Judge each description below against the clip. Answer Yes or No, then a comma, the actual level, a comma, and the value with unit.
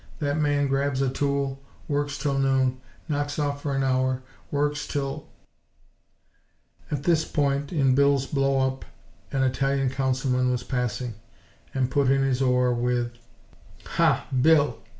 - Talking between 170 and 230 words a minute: No, average, 145 wpm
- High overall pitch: No, low, 135 Hz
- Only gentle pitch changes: Yes, narrow, 1.7 semitones